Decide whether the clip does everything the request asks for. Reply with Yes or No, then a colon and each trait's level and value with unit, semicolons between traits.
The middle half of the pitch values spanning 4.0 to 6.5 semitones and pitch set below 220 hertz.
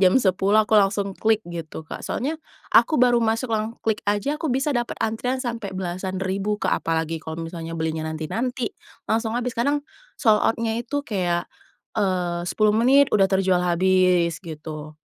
Yes: average, 5.1 semitones; high, 205 Hz